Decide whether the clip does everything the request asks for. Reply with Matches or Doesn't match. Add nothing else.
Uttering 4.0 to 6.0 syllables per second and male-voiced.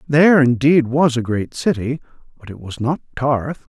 Matches